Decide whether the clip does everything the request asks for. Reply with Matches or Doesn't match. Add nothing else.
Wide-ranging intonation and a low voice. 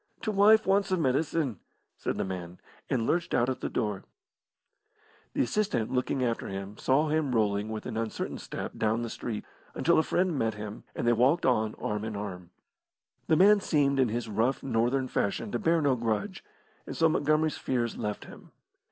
Matches